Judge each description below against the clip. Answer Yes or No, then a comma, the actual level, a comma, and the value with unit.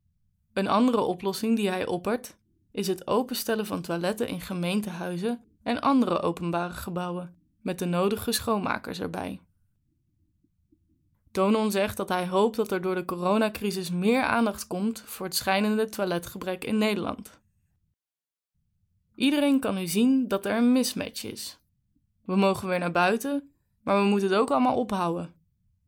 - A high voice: Yes, high, 195 Hz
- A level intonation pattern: No, average, 4.1 semitones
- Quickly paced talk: No, average, 145 wpm